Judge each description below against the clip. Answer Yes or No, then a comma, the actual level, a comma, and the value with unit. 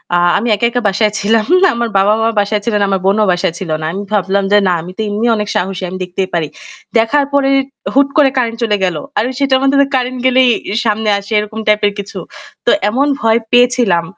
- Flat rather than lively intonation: No, average, 3.9 semitones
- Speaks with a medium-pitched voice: No, high, 215 Hz